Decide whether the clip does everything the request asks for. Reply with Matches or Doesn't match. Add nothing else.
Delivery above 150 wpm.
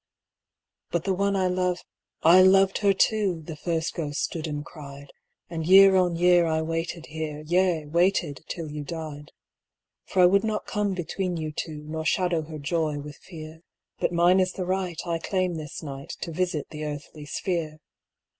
Matches